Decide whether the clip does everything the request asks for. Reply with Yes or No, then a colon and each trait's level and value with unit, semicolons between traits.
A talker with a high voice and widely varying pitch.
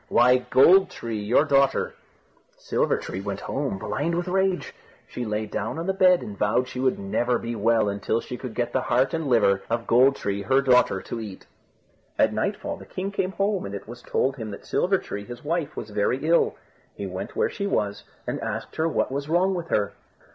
No: low, 125 Hz; wide, 7.5 semitones